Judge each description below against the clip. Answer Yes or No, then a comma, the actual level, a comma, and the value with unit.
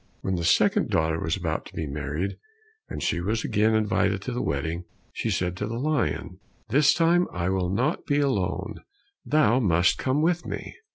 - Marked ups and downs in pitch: Yes, wide, 7.5 semitones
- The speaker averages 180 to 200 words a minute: Yes, average, 185 wpm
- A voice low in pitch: Yes, low, 100 Hz